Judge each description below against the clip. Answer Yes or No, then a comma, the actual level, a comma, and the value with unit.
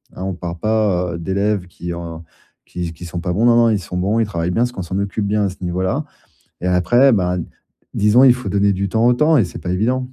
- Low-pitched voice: Yes, low, 100 Hz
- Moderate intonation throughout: Yes, average, 3.9 semitones